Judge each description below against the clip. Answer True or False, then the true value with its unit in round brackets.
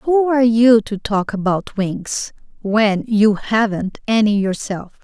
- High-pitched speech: True (215 Hz)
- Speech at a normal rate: False (130 wpm)